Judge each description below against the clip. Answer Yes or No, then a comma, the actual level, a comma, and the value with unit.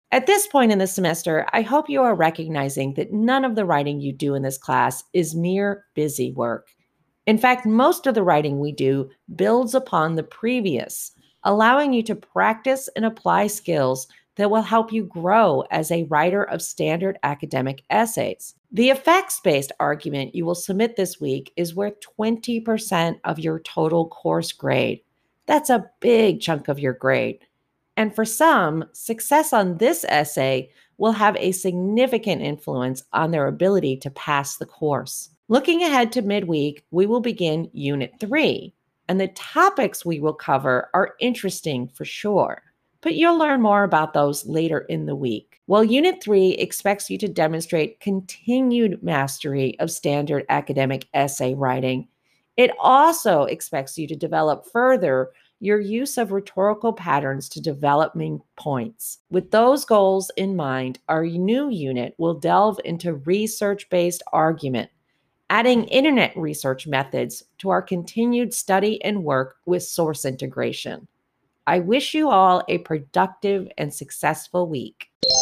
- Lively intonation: Yes, wide, 7.1 semitones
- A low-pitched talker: No, medium, 180 Hz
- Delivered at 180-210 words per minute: No, average, 155 wpm